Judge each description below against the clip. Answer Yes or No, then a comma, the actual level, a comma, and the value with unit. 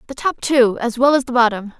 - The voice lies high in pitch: Yes, high, 245 Hz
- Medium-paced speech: No, fast, 270 wpm